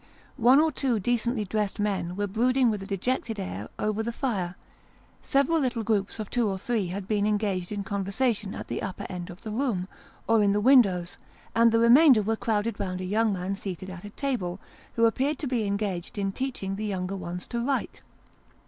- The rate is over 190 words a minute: Yes, average, 200 wpm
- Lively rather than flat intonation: No, average, 3.6 semitones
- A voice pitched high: Yes, high, 210 Hz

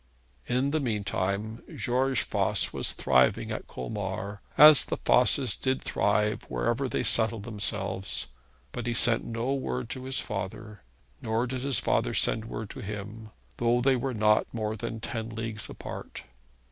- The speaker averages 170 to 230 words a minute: No, average, 160 wpm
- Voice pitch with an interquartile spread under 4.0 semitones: Yes, average, 2.9 semitones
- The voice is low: Yes, low, 115 Hz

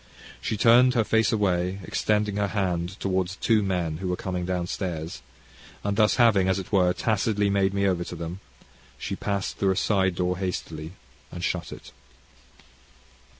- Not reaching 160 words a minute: No, average, 170 wpm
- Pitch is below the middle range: Yes, very low, 95 Hz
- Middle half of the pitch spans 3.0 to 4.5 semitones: No, narrow, 2.4 semitones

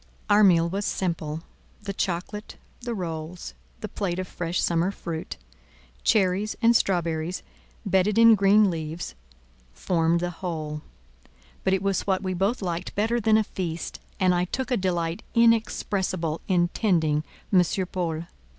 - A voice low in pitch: No, medium, 180 Hz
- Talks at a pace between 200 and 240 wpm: No, average, 145 wpm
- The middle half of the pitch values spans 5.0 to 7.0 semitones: No, average, 3.2 semitones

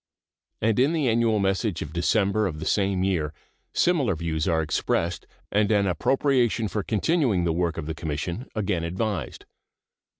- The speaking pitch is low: Yes, very low, 95 Hz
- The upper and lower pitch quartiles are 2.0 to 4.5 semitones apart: No, average, 5.0 semitones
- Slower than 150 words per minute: No, average, 160 wpm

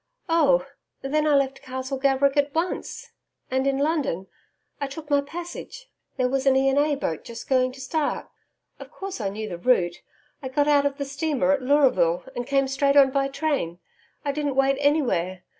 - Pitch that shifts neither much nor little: No, narrow, 1.9 semitones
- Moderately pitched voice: No, very high, 275 Hz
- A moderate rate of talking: Yes, average, 190 wpm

